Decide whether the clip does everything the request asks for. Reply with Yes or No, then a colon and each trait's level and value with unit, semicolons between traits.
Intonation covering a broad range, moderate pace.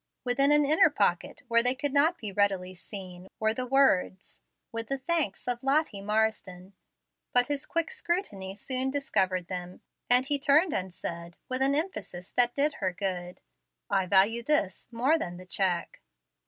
Yes: wide, 6.8 semitones; average, 170 wpm